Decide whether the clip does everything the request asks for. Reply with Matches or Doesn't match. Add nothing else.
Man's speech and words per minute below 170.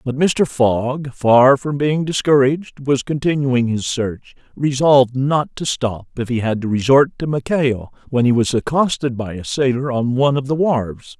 Doesn't match